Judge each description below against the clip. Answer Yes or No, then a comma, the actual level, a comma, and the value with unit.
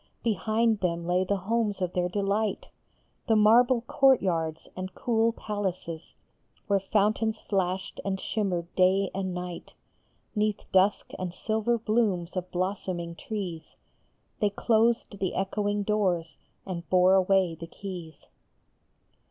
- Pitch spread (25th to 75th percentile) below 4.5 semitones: Yes, average, 3.0 semitones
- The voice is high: Yes, high, 195 Hz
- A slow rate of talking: Yes, slow, 125 wpm